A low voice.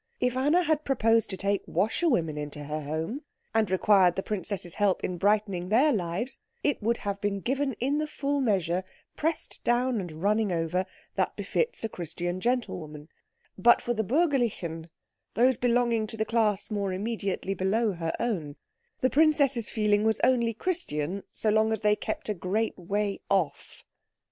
No: high, 210 Hz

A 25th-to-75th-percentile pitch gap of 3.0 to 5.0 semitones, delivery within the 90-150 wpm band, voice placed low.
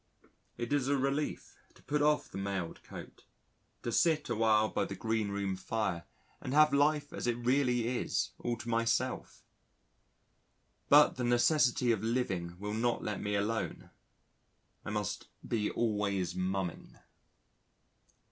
Yes: average, 4.1 semitones; average, 140 wpm; low, 115 Hz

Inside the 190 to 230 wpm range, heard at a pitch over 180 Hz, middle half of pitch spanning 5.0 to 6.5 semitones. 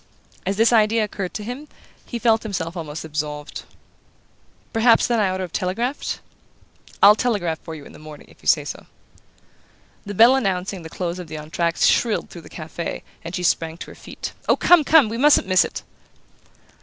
Yes: average, 195 wpm; high, 190 Hz; wide, 5.4 semitones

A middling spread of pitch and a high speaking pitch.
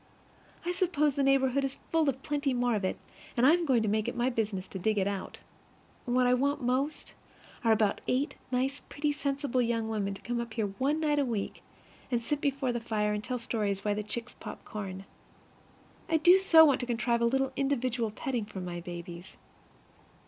Yes: average, 4.6 semitones; high, 245 Hz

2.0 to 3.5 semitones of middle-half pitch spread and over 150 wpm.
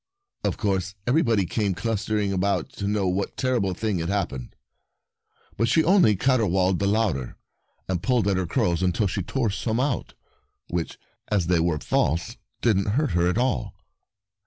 No: average, 3.9 semitones; average, 165 wpm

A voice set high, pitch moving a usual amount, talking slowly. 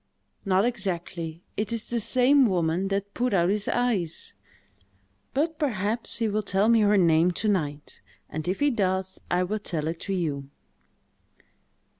No: high, 195 Hz; average, 4.5 semitones; average, 160 wpm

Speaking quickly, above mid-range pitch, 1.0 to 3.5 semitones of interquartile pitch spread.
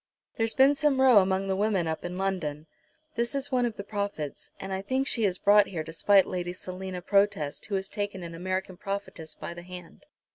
Yes: fast, 215 wpm; high, 195 Hz; average, 2.9 semitones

